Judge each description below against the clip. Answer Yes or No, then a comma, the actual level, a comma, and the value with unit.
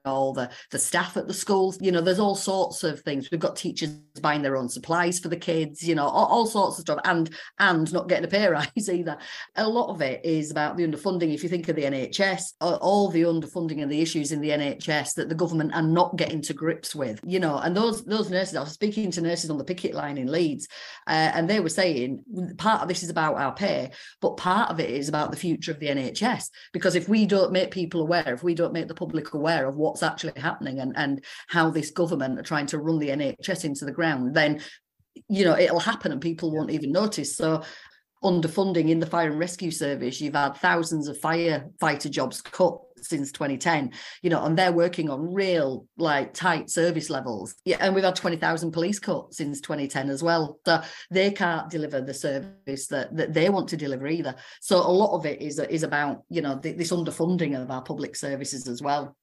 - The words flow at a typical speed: No, fast, 225 wpm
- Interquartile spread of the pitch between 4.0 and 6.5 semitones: No, average, 3.3 semitones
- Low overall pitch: No, medium, 165 Hz